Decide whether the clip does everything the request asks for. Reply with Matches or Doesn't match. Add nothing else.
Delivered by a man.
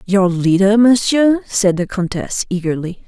Doesn't match